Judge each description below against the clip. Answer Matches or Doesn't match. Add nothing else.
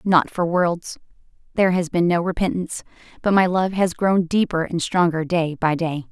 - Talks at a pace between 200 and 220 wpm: Doesn't match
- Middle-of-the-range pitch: Matches